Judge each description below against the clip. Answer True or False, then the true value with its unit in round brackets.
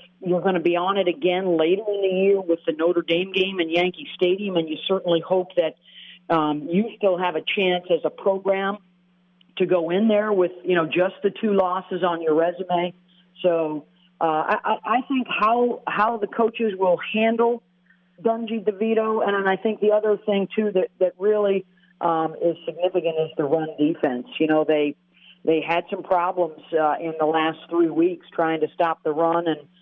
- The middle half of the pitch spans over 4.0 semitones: False (3.1 semitones)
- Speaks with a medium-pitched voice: True (180 Hz)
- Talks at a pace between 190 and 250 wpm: True (195 wpm)